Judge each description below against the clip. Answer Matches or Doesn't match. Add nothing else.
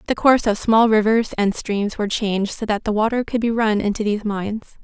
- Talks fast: Matches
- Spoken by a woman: Matches